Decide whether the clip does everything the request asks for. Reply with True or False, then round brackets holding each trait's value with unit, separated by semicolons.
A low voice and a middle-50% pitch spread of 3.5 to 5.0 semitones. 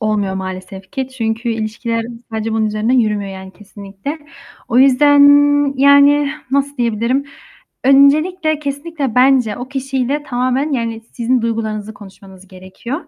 False (235 Hz; 4.5 semitones)